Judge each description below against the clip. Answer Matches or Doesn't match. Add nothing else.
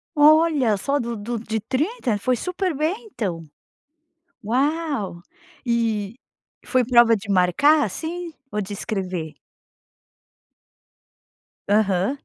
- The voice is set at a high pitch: Matches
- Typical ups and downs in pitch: Doesn't match